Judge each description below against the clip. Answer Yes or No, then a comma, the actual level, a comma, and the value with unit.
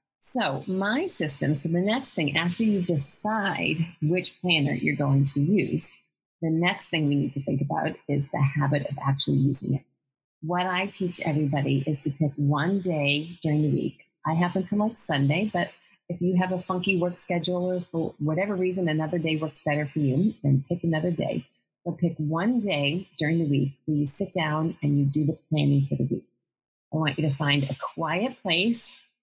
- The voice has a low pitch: No, medium, 160 Hz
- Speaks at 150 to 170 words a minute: No, average, 200 wpm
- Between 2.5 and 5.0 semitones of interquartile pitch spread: Yes, average, 3.8 semitones